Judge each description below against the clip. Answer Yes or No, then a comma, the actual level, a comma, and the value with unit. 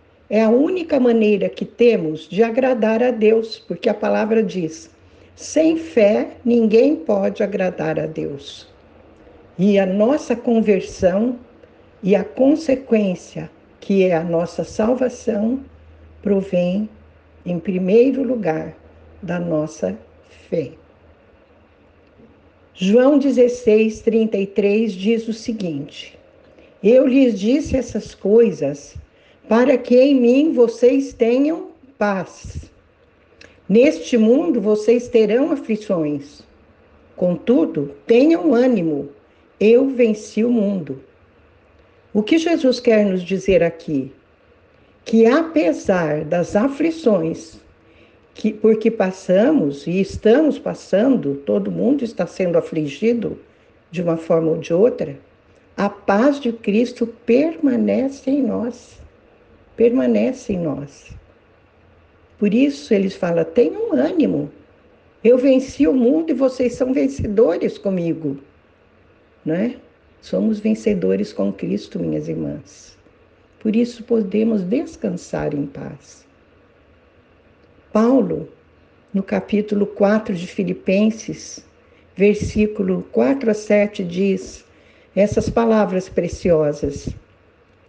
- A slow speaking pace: Yes, slow, 105 wpm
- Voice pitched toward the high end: Yes, high, 215 Hz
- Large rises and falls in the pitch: Yes, wide, 6.0 semitones